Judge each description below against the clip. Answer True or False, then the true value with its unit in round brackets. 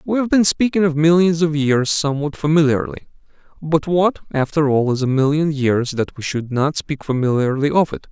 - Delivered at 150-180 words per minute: False (190 wpm)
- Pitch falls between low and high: True (150 Hz)